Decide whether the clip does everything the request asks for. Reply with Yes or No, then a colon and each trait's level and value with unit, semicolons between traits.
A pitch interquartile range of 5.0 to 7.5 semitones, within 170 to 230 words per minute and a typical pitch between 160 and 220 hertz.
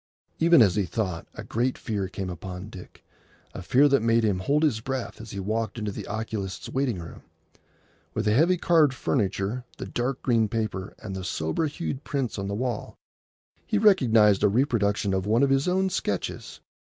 No: average, 5.3 semitones; average, 185 wpm; low, 110 Hz